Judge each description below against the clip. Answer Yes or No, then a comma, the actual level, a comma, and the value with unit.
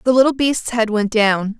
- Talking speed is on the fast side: Yes, fast, 225 wpm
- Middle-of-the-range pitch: No, high, 230 Hz